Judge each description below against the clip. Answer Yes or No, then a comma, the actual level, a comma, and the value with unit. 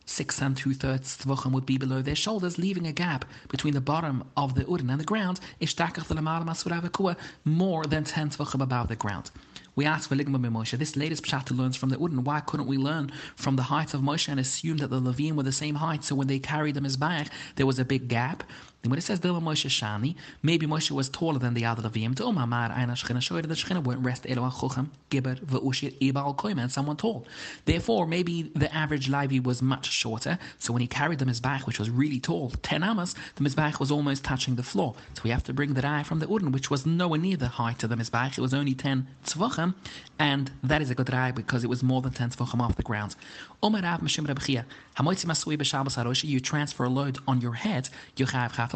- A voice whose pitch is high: No, medium, 140 Hz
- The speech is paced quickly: Yes, fast, 210 wpm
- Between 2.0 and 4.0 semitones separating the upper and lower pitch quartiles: Yes, average, 3.1 semitones